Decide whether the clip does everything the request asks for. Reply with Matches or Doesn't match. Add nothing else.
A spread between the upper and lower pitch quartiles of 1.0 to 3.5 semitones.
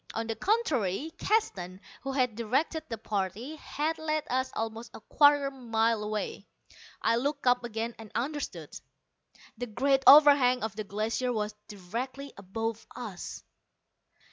Doesn't match